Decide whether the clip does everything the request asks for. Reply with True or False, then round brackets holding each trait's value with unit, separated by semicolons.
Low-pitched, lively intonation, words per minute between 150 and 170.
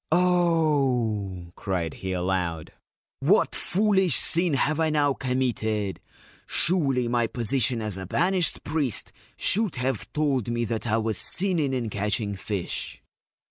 False (125 Hz; 6.8 semitones; 140 wpm)